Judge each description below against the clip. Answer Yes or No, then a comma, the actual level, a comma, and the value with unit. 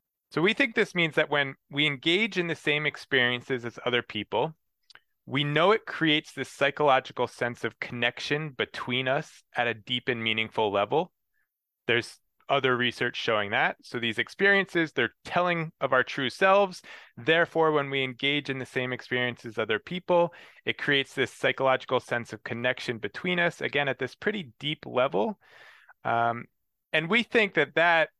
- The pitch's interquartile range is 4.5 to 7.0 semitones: Yes, average, 5.0 semitones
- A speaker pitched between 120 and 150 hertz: Yes, medium, 140 Hz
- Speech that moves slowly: No, average, 170 wpm